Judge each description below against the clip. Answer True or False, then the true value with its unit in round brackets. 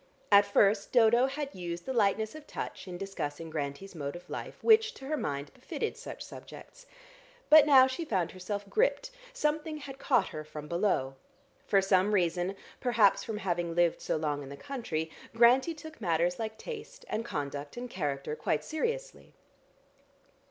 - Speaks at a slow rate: False (165 wpm)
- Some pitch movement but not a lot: False (8.3 semitones)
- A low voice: False (200 Hz)